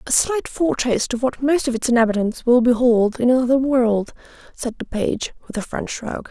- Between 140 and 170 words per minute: No, average, 200 wpm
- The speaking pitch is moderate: No, high, 245 Hz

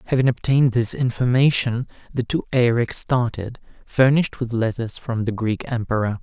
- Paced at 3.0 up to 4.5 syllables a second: No, 5.1 syllables/s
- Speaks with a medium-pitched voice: No, low, 120 Hz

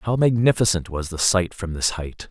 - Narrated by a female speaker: No, male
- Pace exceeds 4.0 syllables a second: Yes, 4.9 syllables/s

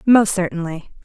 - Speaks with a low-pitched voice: No, high, 190 Hz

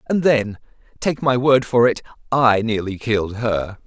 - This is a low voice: Yes, low, 120 Hz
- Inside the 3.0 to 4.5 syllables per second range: Yes, 4.4 syllables/s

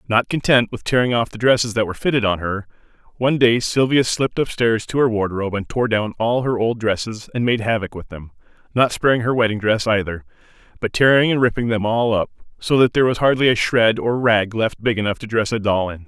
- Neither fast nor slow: No, fast, 230 wpm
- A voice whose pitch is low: Yes, low, 115 Hz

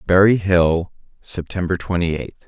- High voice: No, very low, 90 Hz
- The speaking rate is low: Yes, slow, 120 wpm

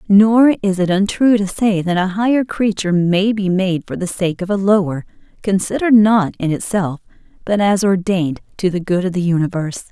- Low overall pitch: No, high, 190 Hz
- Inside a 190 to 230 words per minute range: Yes, average, 195 wpm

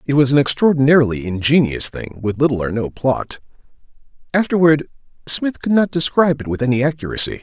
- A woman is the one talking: No, male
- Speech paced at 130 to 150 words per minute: No, average, 160 wpm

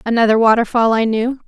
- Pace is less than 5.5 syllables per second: No, 5.8 syllables/s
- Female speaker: Yes, female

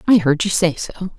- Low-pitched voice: No, medium, 175 Hz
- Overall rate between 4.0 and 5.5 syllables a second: Yes, 5.0 syllables/s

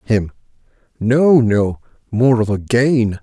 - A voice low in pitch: Yes, low, 115 Hz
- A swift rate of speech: No, slow, 130 wpm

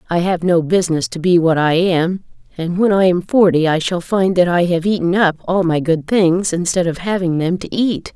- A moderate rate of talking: No, fast, 235 wpm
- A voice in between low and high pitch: Yes, medium, 175 Hz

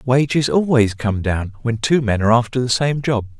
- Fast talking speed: Yes, fast, 210 wpm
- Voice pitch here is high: No, low, 120 Hz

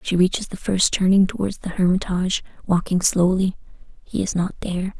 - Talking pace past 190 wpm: No, average, 155 wpm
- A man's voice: No, female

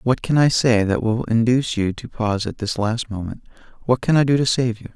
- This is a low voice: Yes, low, 115 Hz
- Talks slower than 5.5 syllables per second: No, 5.7 syllables/s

